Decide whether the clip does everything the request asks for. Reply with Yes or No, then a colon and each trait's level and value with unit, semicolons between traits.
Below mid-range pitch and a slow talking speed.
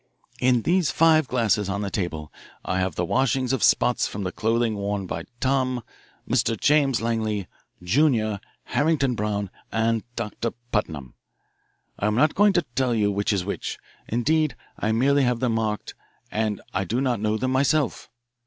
No: low, 115 Hz; average, 165 wpm